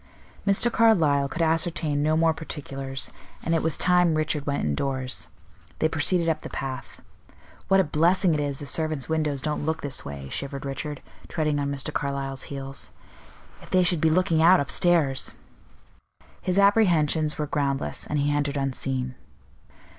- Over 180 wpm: No, average, 160 wpm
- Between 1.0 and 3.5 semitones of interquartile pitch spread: Yes, average, 3.0 semitones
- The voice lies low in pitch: No, medium, 150 Hz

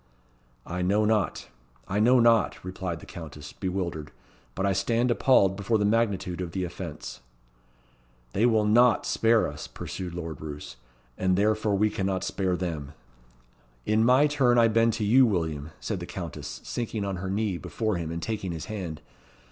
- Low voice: Yes, low, 100 Hz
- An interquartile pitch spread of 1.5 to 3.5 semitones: No, average, 4.2 semitones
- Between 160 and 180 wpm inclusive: Yes, average, 170 wpm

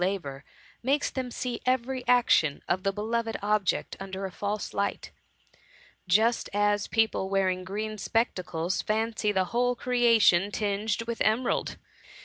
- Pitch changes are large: No, average, 3.3 semitones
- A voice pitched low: No, high, 210 Hz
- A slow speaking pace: Yes, slow, 130 wpm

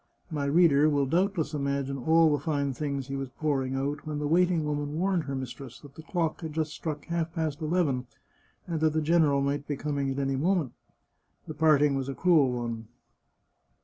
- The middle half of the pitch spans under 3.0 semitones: Yes, narrow, 2.6 semitones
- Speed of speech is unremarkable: No, fast, 210 wpm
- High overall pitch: No, medium, 145 Hz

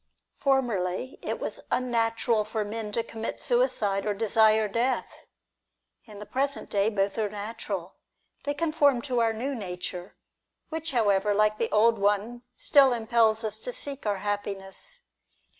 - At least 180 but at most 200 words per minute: No, average, 145 wpm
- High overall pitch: Yes, high, 220 Hz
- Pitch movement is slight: No, average, 3.5 semitones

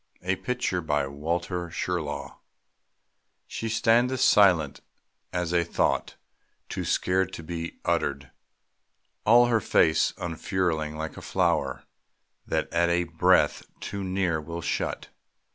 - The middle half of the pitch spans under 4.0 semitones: Yes, average, 2.9 semitones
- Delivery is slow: Yes, slow, 120 wpm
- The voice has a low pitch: Yes, very low, 85 Hz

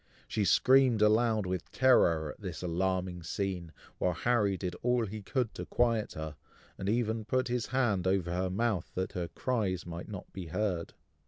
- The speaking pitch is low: Yes, low, 100 Hz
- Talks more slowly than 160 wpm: No, average, 175 wpm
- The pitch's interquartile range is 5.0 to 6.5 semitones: No, average, 4.5 semitones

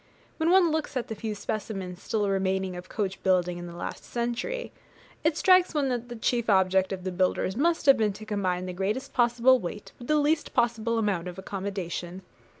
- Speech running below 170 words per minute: No, average, 200 wpm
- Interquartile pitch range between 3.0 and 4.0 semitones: No, average, 4.8 semitones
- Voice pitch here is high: Yes, high, 210 Hz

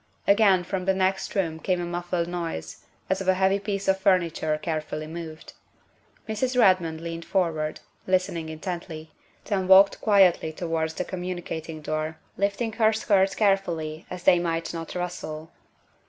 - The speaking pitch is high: No, medium, 175 Hz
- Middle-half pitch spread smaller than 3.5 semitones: Yes, average, 3.1 semitones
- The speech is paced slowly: No, average, 150 wpm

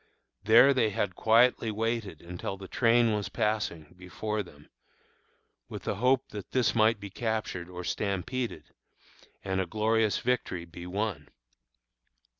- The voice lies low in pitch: Yes, low, 105 Hz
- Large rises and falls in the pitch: No, average, 3.7 semitones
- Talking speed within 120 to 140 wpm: Yes, slow, 135 wpm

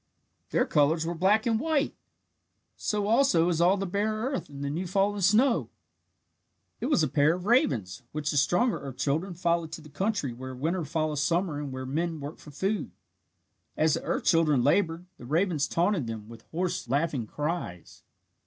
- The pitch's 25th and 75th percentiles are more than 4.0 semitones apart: Yes, average, 5.3 semitones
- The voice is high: No, medium, 165 Hz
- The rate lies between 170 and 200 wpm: Yes, average, 180 wpm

